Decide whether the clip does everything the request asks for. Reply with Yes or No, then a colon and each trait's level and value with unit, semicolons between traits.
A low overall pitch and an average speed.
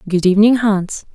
No: high, 205 Hz; average, 155 wpm